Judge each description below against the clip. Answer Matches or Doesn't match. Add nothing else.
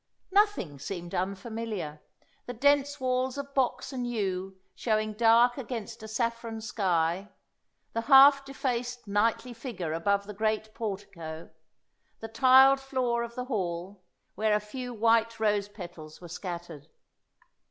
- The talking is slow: Matches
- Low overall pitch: Doesn't match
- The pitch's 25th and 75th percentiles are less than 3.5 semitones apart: Doesn't match